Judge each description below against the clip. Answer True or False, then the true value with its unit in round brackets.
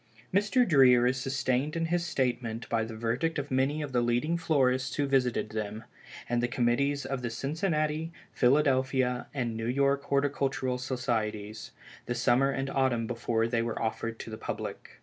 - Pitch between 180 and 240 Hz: False (130 Hz)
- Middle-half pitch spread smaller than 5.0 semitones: True (3.0 semitones)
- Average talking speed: True (170 wpm)